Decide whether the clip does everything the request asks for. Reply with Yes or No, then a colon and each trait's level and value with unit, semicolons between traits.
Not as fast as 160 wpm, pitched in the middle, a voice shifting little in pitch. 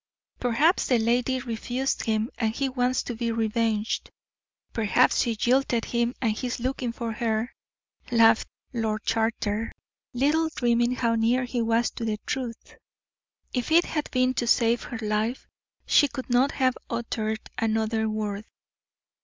No: average, 150 wpm; high, 235 Hz; narrow, 2.1 semitones